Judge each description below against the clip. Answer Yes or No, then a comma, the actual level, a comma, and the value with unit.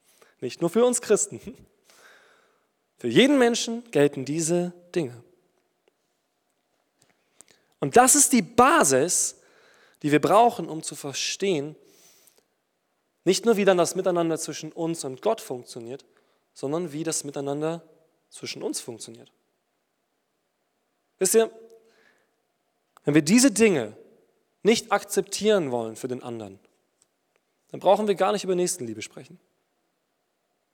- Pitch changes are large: Yes, wide, 6.6 semitones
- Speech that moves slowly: Yes, slow, 115 wpm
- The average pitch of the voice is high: No, medium, 180 Hz